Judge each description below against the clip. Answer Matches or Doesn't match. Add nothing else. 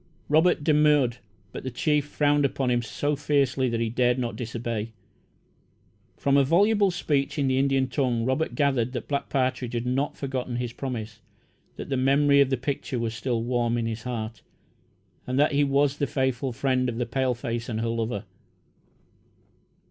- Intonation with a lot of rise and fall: Doesn't match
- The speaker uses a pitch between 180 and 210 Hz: Doesn't match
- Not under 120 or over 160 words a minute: Doesn't match